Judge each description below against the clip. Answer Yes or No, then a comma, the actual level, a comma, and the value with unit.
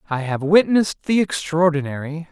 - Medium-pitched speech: Yes, medium, 165 Hz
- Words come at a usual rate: No, slow, 130 wpm